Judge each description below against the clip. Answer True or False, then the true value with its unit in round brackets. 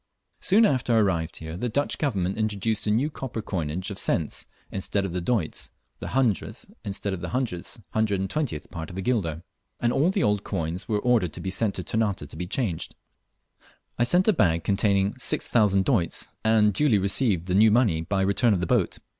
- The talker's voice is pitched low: True (100 Hz)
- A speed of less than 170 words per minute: False (190 wpm)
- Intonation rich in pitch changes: False (4.7 semitones)